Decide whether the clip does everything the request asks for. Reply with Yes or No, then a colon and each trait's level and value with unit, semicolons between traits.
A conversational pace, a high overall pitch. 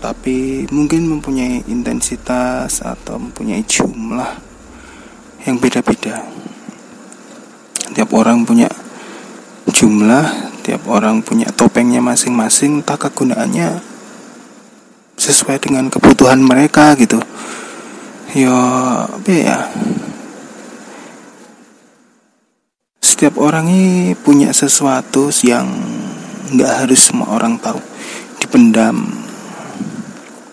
No: slow, 80 wpm; high, 205 Hz